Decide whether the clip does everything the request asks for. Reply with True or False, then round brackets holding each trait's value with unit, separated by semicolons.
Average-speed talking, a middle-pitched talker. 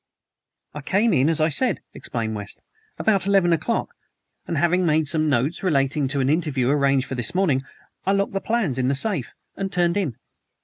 True (190 wpm; 155 Hz)